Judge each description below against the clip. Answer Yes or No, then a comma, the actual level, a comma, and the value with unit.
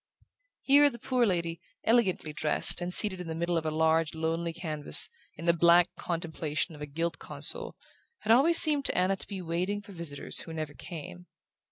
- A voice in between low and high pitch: Yes, medium, 170 Hz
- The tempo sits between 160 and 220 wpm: Yes, average, 190 wpm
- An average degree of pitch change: Yes, average, 3.3 semitones